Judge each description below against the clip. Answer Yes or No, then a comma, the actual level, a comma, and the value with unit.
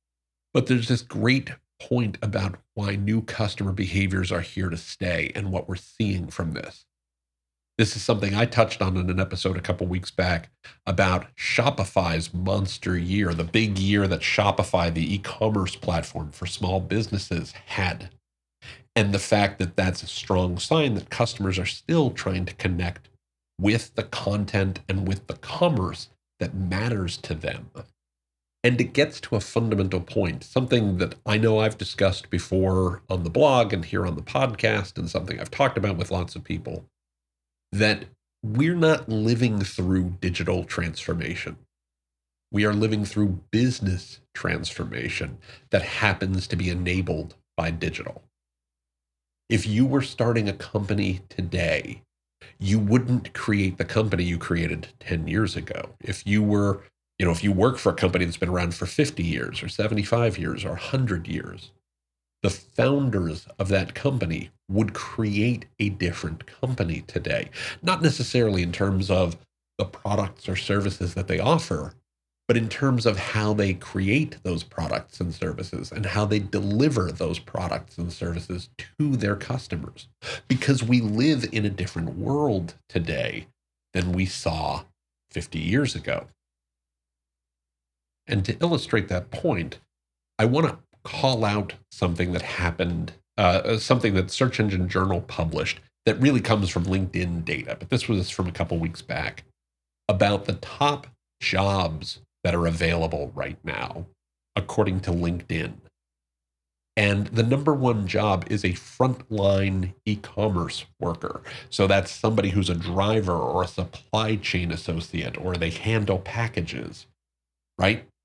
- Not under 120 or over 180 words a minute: Yes, average, 150 wpm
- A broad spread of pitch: No, average, 4.2 semitones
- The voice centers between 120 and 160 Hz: No, very low, 95 Hz